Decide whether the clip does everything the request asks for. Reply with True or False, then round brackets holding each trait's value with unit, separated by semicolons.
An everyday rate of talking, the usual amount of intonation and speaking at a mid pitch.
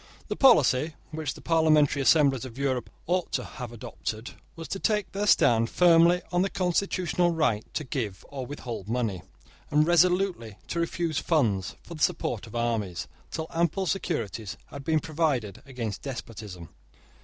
False (155 wpm; 6.6 semitones; 145 Hz)